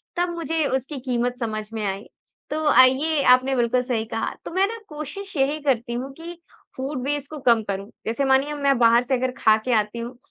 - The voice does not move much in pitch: No, average, 3.9 semitones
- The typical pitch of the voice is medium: No, very high, 260 Hz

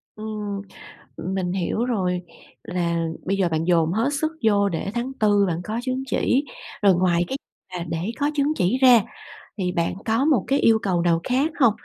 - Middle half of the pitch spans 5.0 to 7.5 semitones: Yes, wide, 5.5 semitones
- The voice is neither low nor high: No, high, 200 Hz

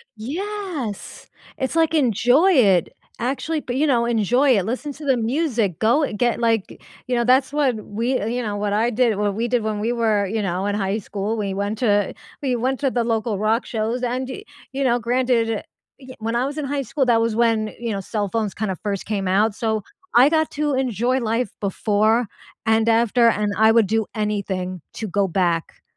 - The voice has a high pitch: Yes, high, 230 Hz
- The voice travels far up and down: No, average, 3.4 semitones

